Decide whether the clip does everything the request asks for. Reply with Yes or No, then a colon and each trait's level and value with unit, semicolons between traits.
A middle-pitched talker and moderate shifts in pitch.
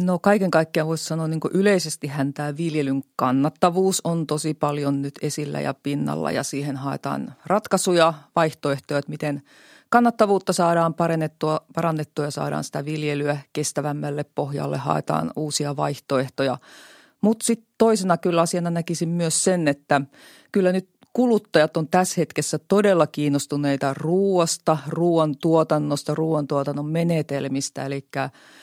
Yes: medium, 155 Hz; average, 3.6 semitones